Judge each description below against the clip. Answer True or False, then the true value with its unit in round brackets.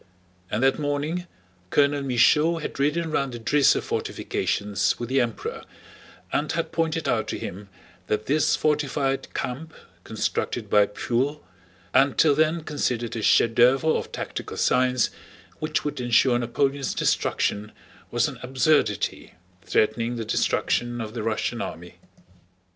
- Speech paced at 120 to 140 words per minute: True (135 wpm)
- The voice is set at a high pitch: False (135 Hz)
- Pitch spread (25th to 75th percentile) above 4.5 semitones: False (4.2 semitones)